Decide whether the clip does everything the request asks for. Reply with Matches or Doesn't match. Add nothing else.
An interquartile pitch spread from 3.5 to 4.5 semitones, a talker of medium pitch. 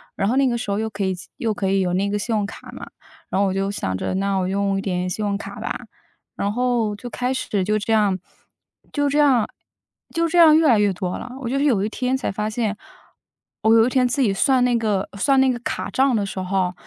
Doesn't match